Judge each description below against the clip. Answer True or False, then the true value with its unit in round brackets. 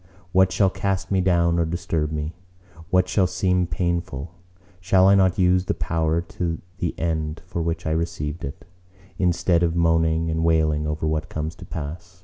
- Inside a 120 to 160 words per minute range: False (175 wpm)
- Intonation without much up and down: True (2.2 semitones)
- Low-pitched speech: True (85 Hz)